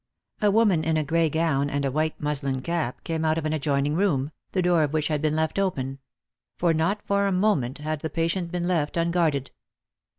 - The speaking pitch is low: No, medium, 160 Hz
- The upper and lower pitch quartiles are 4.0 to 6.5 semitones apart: No, average, 2.9 semitones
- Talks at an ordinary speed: No, fast, 210 wpm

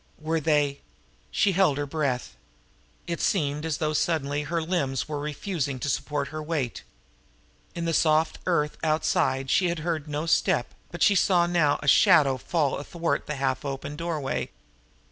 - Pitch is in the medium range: Yes, medium, 150 Hz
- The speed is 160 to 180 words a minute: Yes, average, 165 wpm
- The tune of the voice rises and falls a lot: No, average, 2.8 semitones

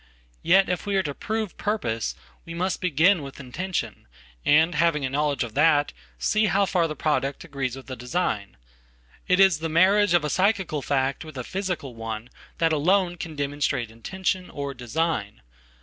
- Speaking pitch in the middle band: Yes, medium, 155 Hz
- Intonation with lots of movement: Yes, wide, 5.7 semitones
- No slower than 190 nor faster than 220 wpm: No, average, 160 wpm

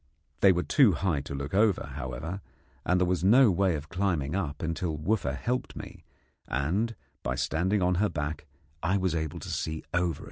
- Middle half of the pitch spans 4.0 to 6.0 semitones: Yes, average, 4.4 semitones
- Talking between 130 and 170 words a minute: No, average, 185 wpm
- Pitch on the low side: Yes, very low, 90 Hz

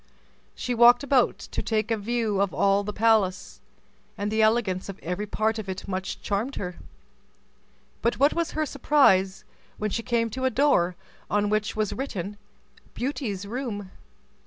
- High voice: Yes, high, 215 Hz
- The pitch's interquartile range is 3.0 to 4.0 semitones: Yes, average, 3.5 semitones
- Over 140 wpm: Yes, average, 160 wpm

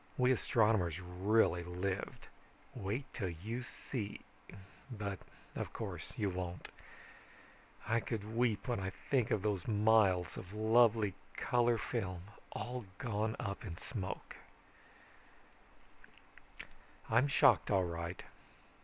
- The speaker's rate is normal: No, slow, 110 wpm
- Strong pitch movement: No, average, 3.8 semitones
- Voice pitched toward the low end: Yes, low, 105 Hz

